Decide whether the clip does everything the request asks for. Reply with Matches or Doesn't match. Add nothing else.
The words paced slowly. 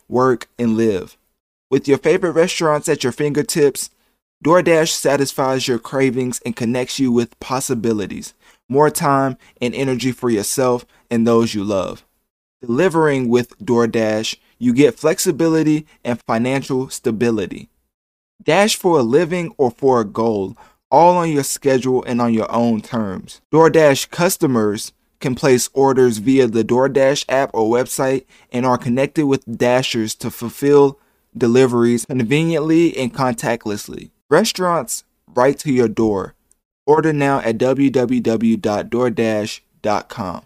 Matches